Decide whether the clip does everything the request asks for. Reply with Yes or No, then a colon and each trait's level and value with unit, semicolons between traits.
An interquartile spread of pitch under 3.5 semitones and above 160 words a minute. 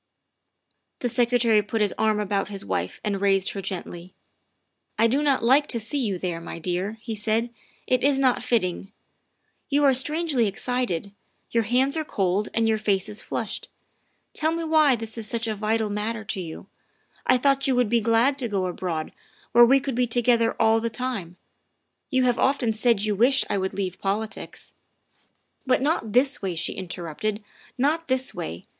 No: average, 4.2 semitones; average, 200 wpm